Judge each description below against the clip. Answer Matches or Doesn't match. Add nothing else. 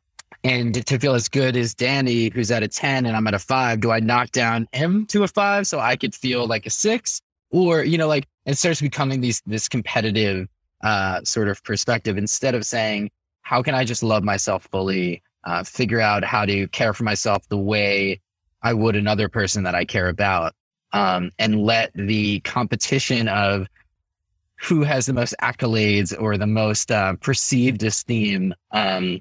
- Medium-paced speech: Matches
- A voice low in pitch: Matches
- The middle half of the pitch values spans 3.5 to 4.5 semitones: Matches